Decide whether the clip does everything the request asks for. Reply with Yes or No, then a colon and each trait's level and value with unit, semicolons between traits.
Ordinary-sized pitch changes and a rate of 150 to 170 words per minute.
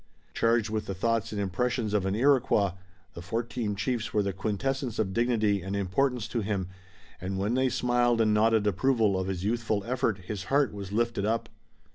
No: average, 3.3 semitones; average, 185 wpm